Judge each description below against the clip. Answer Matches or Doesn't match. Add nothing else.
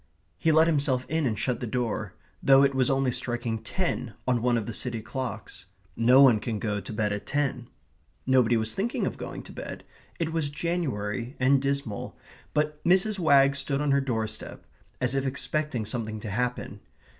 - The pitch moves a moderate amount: Matches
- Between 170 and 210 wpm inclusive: Matches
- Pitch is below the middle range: Matches